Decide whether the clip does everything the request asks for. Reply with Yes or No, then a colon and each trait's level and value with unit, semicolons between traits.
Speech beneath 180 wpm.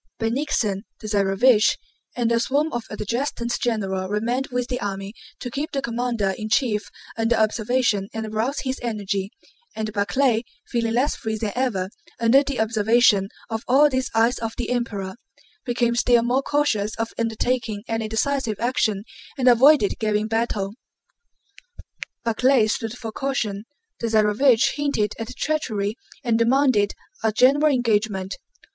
Yes: average, 145 wpm